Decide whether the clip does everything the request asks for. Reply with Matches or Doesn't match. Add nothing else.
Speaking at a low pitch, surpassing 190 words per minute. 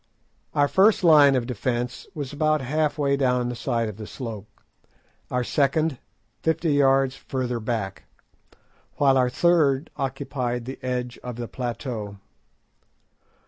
Doesn't match